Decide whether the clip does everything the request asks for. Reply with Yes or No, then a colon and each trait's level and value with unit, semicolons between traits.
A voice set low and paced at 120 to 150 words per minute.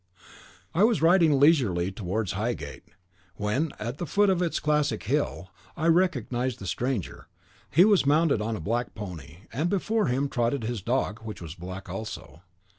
No: low, 120 Hz; average, 165 wpm